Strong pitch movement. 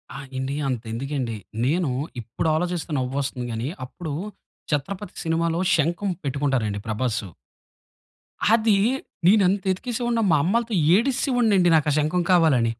Yes: wide, 6.4 semitones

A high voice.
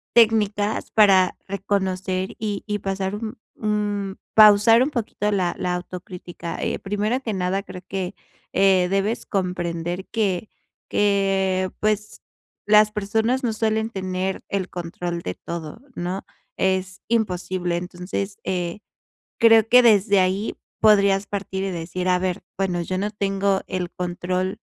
Yes: high, 195 Hz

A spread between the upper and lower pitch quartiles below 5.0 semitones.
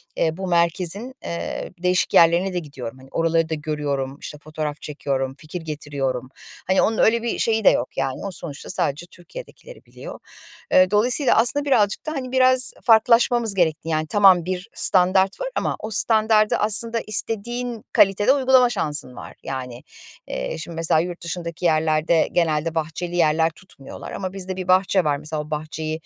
No: wide, 5.6 semitones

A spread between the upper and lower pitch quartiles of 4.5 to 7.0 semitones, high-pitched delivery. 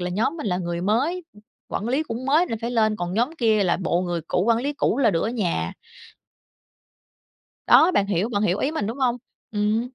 Yes: average, 5.1 semitones; high, 220 Hz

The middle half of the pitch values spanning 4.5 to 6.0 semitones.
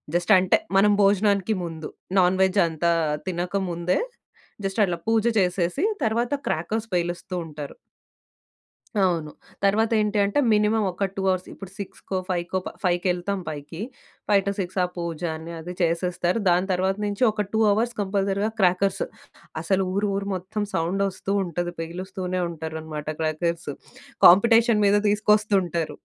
No: average, 2.8 semitones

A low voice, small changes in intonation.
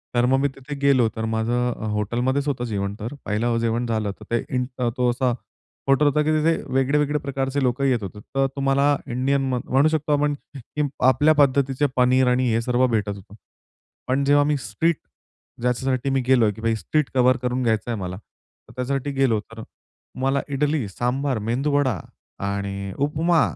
No: low, 130 Hz; average, 3.3 semitones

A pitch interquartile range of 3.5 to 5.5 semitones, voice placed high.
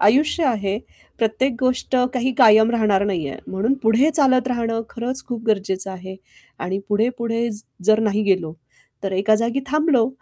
Yes: average, 3.8 semitones; high, 225 Hz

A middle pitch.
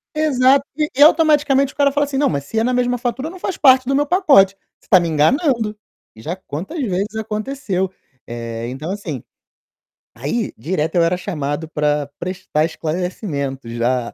No: high, 195 Hz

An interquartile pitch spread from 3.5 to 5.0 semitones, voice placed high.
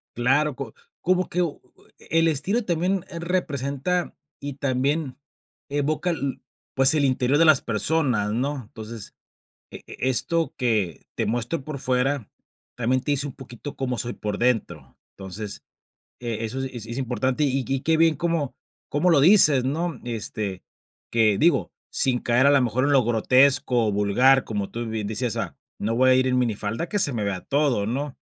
No: average, 4.0 semitones; low, 130 Hz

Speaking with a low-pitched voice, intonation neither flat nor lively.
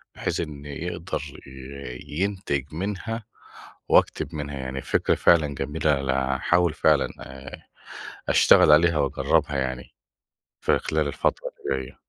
Yes: very low, 75 Hz; average, 3.5 semitones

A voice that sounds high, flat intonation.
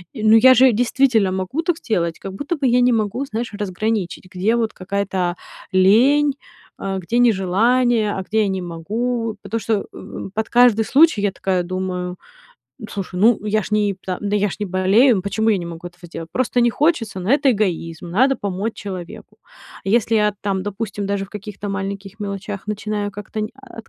No: high, 205 Hz; average, 3.2 semitones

